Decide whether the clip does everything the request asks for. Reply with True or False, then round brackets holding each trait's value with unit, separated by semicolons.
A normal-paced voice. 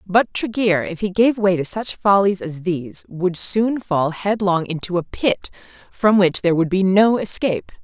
True (190 wpm)